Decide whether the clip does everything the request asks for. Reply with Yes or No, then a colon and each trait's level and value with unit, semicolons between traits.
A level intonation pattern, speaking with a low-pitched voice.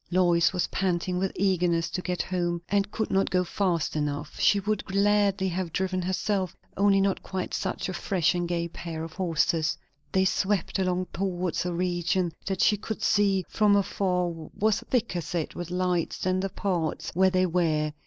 No: narrow, 2.0 semitones; medium, 185 Hz